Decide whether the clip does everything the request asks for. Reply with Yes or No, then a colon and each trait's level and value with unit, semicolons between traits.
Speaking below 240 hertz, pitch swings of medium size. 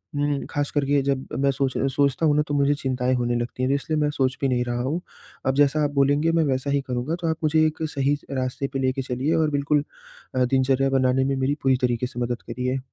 No: low, 135 Hz; narrow, 2.0 semitones